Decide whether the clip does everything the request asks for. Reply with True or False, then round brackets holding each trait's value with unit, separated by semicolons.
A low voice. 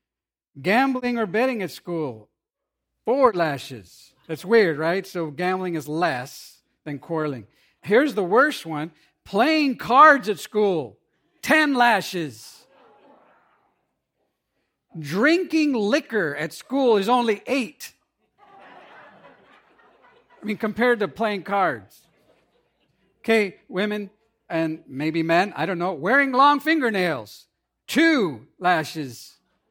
False (190 Hz)